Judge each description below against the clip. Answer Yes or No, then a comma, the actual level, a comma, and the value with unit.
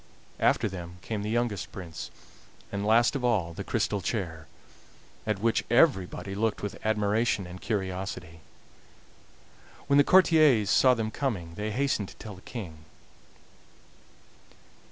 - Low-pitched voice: Yes, low, 105 Hz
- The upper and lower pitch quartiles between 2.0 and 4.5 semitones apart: Yes, average, 4.1 semitones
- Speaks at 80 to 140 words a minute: Yes, slow, 135 wpm